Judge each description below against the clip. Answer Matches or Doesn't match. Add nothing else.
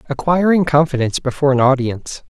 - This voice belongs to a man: Matches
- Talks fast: Doesn't match